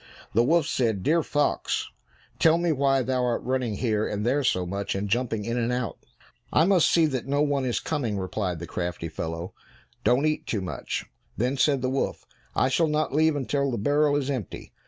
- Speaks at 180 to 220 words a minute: Yes, average, 200 wpm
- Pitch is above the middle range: No, low, 130 Hz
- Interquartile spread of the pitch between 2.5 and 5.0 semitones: No, wide, 5.6 semitones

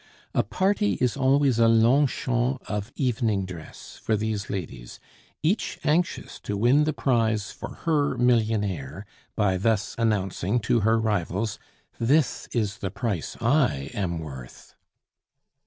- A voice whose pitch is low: Yes, low, 115 Hz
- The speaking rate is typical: No, slow, 130 wpm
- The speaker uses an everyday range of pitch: Yes, average, 4.5 semitones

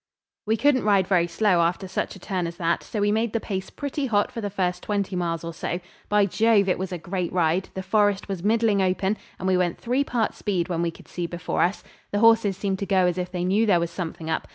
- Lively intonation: No, average, 2.8 semitones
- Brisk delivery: Yes, fast, 255 wpm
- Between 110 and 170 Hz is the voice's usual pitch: No, high, 190 Hz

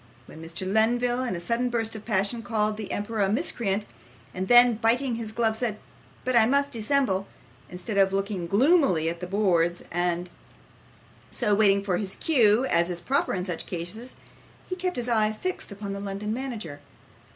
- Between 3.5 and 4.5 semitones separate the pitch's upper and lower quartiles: Yes, average, 4.2 semitones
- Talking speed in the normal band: Yes, average, 180 wpm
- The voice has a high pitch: Yes, high, 215 Hz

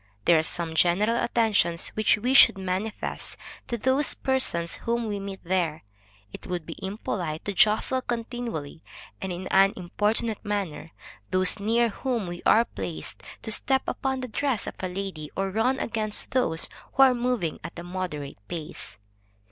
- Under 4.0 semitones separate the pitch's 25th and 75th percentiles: No, average, 5.2 semitones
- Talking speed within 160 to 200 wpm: Yes, average, 165 wpm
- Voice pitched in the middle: No, high, 200 Hz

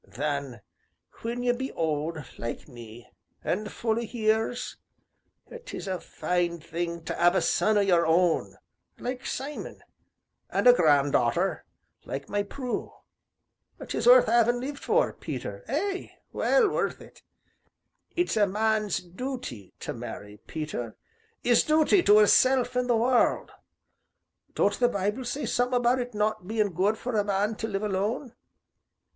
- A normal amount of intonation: No, wide, 6.2 semitones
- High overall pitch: Yes, high, 215 Hz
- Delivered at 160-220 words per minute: No, average, 145 wpm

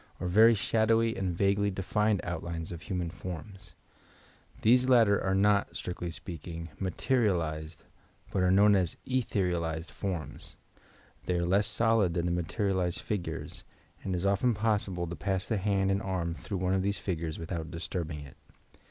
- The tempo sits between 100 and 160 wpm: No, average, 175 wpm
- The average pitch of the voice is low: Yes, very low, 95 Hz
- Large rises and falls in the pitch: No, average, 3.0 semitones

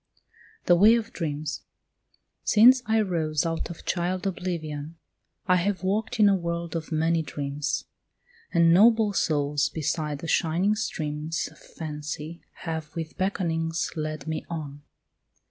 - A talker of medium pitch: Yes, medium, 165 Hz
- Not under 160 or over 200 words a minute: No, slow, 135 wpm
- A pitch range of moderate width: Yes, average, 3.3 semitones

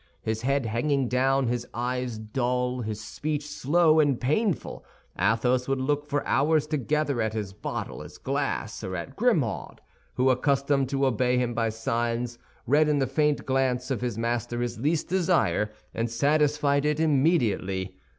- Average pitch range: Yes, average, 3.7 semitones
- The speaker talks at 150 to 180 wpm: Yes, average, 160 wpm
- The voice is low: Yes, low, 130 Hz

